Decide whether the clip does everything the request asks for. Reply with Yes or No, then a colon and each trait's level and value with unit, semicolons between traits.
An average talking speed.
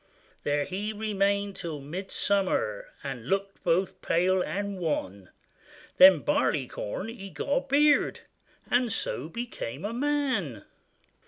No: slow, 115 wpm